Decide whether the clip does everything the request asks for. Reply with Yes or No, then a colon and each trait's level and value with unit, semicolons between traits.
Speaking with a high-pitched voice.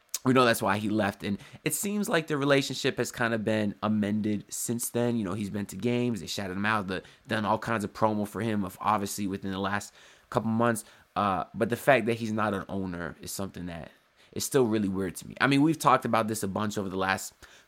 No: low, 105 Hz